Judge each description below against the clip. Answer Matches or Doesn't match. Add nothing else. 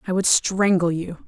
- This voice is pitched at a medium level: Matches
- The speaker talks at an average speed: Matches